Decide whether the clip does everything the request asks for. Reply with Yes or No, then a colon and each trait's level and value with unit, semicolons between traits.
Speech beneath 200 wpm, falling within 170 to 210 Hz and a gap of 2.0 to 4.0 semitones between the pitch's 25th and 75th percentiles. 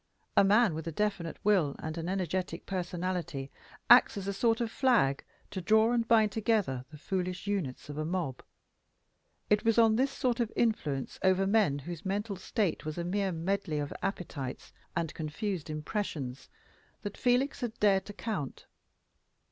No: average, 165 wpm; high, 190 Hz; average, 5.2 semitones